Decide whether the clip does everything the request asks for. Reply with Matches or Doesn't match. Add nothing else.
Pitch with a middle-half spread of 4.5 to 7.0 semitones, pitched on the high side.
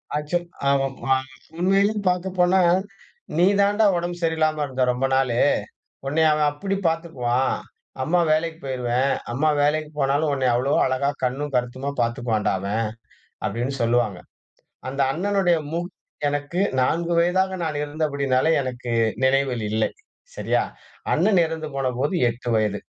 Doesn't match